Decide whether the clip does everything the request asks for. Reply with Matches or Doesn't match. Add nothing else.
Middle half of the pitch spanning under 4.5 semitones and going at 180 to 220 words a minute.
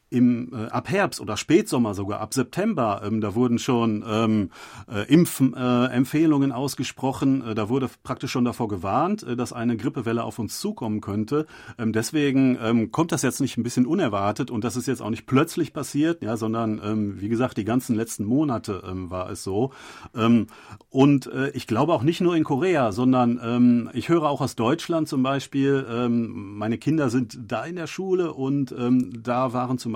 Matches